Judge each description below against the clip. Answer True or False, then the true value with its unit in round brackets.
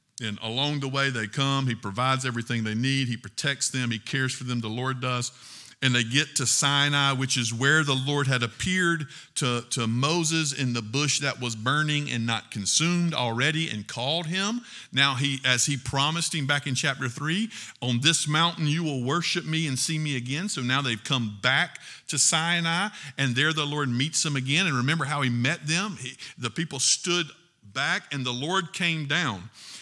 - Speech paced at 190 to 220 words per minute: True (200 wpm)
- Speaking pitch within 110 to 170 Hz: True (140 Hz)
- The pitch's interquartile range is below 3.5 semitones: False (4.1 semitones)